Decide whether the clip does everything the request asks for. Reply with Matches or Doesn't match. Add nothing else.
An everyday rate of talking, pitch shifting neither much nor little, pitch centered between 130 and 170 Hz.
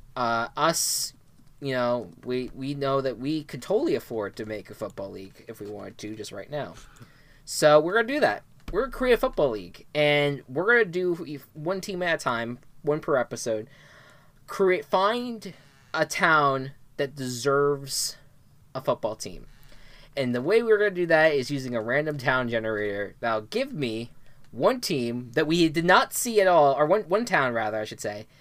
Matches